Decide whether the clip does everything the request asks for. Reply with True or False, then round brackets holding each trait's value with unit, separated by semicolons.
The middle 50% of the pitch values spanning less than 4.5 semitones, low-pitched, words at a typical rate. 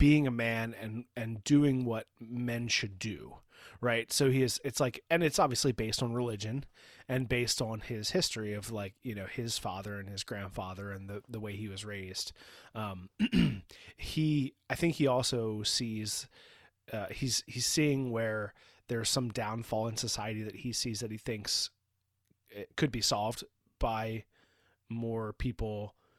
True (2.9 semitones; 115 Hz; 165 wpm)